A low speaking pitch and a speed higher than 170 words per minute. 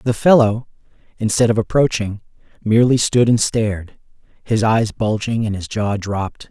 No: low, 110 Hz; average, 150 wpm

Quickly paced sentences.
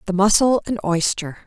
No: average, 165 wpm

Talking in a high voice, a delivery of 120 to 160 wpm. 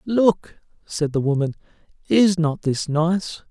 No: medium, 165 Hz; slow, 135 wpm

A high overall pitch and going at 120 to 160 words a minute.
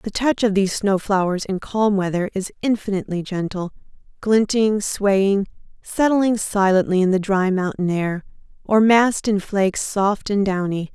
Yes: high, 200 Hz; average, 150 wpm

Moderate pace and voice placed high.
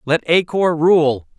No: average, 175 wpm; medium, 160 Hz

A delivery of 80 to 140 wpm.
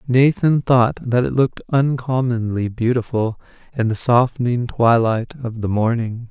Yes: slow, 135 wpm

